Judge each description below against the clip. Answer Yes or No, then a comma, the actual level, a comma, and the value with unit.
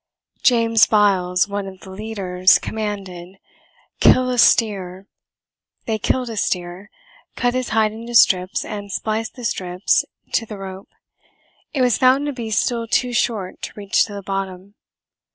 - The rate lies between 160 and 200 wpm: No, average, 150 wpm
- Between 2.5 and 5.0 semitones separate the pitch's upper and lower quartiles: Yes, average, 3.3 semitones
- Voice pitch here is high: Yes, high, 210 Hz